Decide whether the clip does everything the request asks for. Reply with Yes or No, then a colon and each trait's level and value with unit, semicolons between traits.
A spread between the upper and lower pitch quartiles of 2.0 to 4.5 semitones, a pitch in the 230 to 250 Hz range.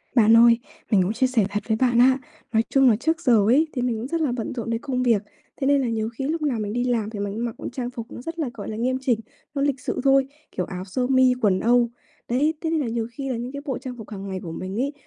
Yes: average, 3.3 semitones; high, 240 Hz